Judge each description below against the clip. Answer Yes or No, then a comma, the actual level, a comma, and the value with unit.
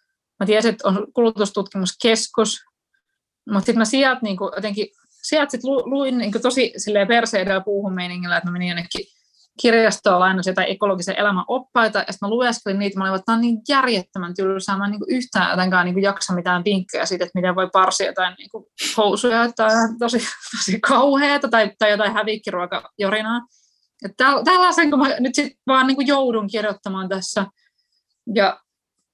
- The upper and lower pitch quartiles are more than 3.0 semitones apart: Yes, average, 4.1 semitones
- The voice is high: Yes, high, 215 Hz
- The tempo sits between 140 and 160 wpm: Yes, average, 150 wpm